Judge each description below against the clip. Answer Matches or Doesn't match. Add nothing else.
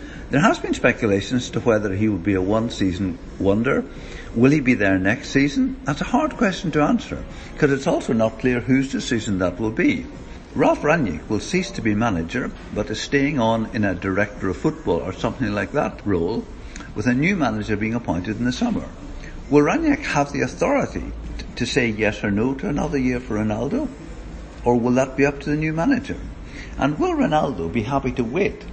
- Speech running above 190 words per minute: Matches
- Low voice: Matches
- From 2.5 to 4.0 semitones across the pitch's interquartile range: Doesn't match